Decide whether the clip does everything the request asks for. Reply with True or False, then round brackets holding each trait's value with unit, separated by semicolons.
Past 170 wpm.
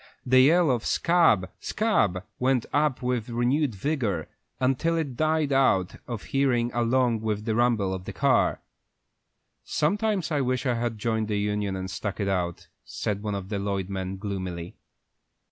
False (160 wpm)